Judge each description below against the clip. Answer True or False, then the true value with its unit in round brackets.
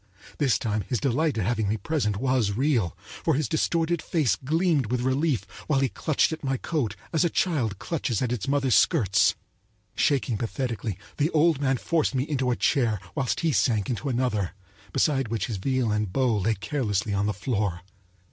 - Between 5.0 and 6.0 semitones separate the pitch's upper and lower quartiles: True (5.3 semitones)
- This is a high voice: False (130 Hz)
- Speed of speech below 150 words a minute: False (185 wpm)